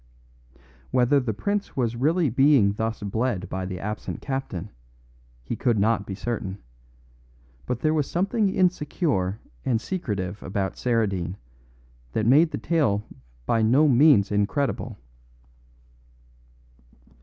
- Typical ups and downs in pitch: No, wide, 6.4 semitones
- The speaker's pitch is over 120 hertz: No, low, 115 Hz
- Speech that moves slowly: Yes, slow, 120 wpm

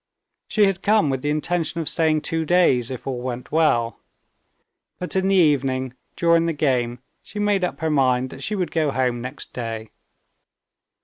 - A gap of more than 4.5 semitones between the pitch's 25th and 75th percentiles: Yes, average, 5.1 semitones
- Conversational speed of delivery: Yes, average, 180 wpm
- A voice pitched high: No, medium, 150 Hz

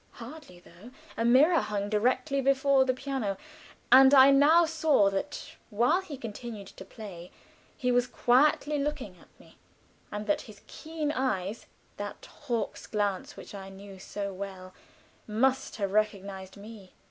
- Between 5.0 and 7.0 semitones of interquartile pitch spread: Yes, wide, 5.5 semitones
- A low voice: No, high, 230 Hz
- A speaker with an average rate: Yes, average, 145 wpm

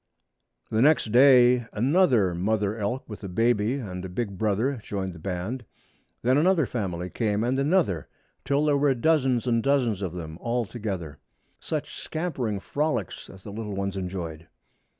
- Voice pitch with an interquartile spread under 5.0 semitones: No, average, 5.3 semitones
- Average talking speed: Yes, average, 160 wpm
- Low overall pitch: Yes, low, 110 Hz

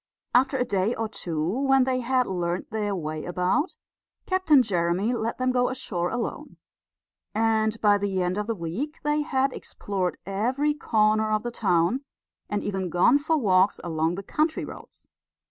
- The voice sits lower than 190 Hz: No, high, 215 Hz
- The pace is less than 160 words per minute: No, average, 165 wpm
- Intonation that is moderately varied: No, wide, 5.7 semitones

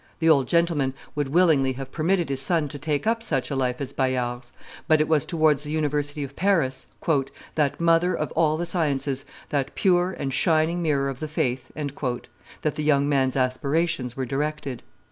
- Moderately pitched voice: Yes, medium, 145 Hz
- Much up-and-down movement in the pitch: No, average, 3.3 semitones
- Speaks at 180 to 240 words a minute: Yes, average, 185 wpm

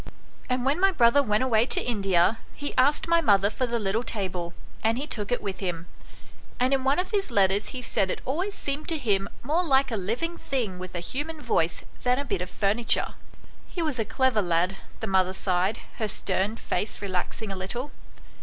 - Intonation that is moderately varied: No, wide, 6.0 semitones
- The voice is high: Yes, high, 225 Hz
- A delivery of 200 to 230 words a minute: Yes, fast, 205 wpm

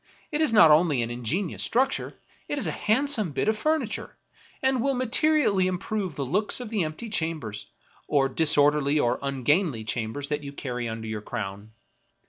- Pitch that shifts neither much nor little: No, wide, 8.9 semitones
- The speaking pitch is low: No, medium, 155 Hz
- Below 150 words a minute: No, average, 175 wpm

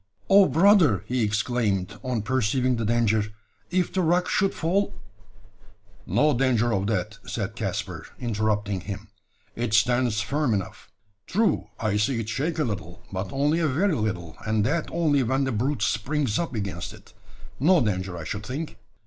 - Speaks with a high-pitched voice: No, low, 115 Hz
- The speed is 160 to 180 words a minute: Yes, average, 165 wpm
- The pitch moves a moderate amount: No, wide, 6.0 semitones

